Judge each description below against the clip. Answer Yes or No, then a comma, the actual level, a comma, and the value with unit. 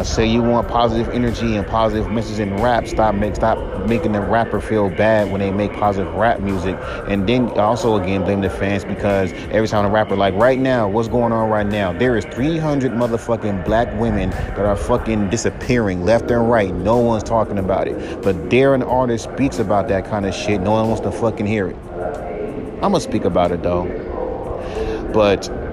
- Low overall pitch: Yes, low, 110 Hz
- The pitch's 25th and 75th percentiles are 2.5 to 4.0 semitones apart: Yes, average, 2.8 semitones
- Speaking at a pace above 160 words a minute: Yes, average, 200 wpm